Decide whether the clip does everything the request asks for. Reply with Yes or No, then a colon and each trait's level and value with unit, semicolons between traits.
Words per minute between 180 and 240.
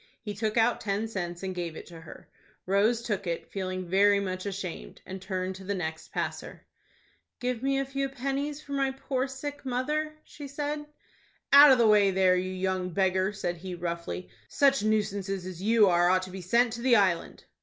Yes: average, 195 wpm